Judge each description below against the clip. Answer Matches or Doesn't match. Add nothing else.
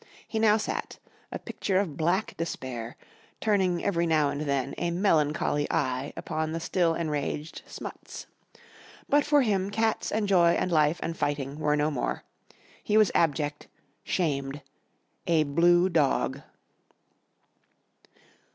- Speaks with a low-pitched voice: Doesn't match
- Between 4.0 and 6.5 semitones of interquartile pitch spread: Matches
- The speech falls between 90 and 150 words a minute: Matches